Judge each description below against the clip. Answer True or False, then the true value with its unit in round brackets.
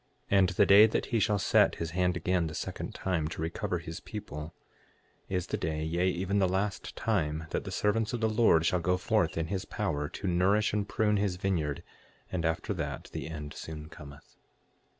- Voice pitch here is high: False (90 Hz)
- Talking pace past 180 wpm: True (205 wpm)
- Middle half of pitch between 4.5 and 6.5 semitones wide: False (3.9 semitones)